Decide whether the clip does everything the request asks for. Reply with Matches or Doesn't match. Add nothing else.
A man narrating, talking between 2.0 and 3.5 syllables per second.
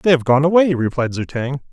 Doesn't match